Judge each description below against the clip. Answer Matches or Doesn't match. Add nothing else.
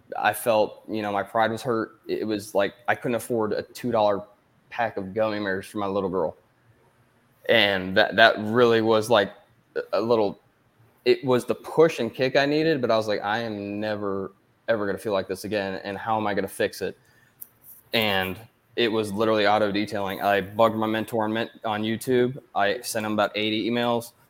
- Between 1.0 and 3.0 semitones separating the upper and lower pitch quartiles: Matches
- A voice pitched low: Matches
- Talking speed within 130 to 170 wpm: Doesn't match